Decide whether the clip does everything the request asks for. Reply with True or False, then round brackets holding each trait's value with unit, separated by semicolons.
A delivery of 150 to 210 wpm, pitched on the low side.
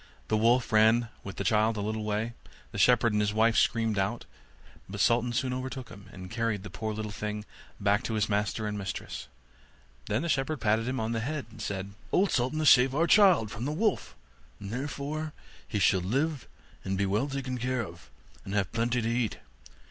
True (205 wpm; 115 Hz)